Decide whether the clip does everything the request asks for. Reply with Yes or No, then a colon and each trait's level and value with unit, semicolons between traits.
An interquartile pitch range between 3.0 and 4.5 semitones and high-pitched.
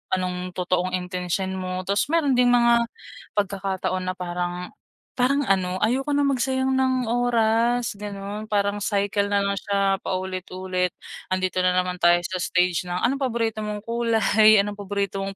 Yes: average, 4.1 semitones; high, 200 Hz